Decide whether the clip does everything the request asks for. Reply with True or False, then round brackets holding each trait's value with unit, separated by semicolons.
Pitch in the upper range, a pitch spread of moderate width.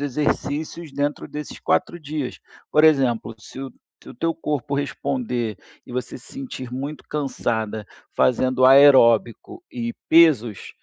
False (140 Hz; 3.6 semitones)